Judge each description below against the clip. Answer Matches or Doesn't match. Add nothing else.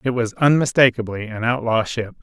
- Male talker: Matches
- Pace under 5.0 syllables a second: Doesn't match